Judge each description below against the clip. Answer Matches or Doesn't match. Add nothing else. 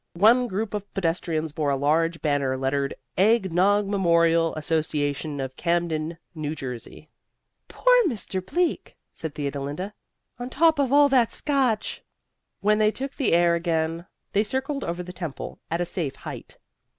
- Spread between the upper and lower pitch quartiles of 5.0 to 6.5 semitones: Matches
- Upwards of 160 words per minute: Doesn't match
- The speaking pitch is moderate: Matches